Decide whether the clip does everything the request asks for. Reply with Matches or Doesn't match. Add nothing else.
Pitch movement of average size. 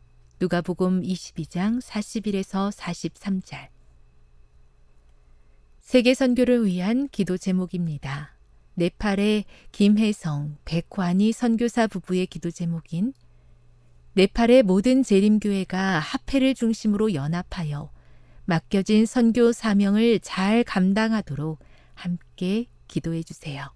Doesn't match